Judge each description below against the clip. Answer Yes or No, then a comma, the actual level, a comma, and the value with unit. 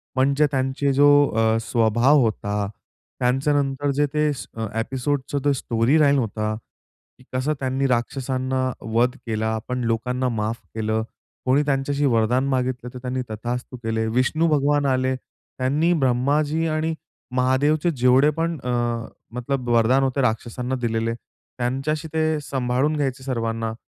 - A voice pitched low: Yes, low, 130 Hz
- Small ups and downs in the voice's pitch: No, average, 3.1 semitones